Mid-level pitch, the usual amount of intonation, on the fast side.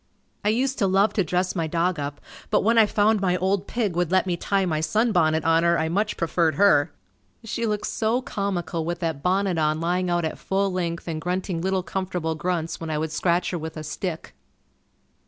Yes: medium, 180 Hz; average, 3.3 semitones; fast, 210 wpm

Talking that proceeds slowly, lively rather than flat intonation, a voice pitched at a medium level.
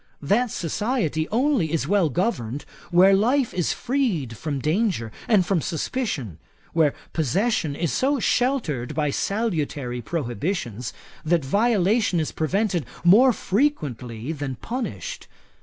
Yes: slow, 120 wpm; wide, 7.7 semitones; medium, 175 Hz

